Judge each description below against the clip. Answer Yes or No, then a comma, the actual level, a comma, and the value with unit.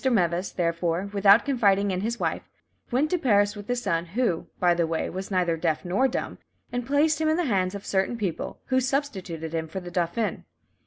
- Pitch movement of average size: No, wide, 5.9 semitones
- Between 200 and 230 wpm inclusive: Yes, fast, 205 wpm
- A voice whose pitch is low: No, high, 195 Hz